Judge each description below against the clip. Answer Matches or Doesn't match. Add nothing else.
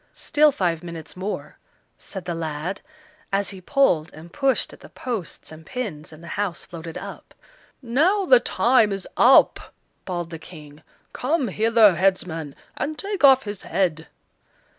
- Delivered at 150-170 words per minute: Matches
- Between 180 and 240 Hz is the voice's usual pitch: Matches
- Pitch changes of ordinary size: Doesn't match